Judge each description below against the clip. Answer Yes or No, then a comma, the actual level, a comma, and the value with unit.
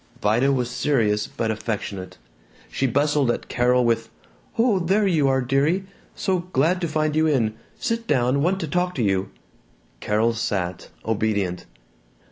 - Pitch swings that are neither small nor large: No, wide, 6.4 semitones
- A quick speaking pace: No, average, 150 wpm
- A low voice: Yes, low, 130 Hz